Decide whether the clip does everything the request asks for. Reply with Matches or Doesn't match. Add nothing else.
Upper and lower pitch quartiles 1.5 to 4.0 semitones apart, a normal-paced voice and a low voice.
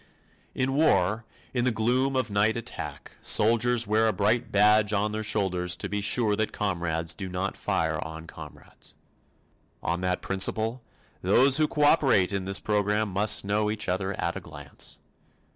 Matches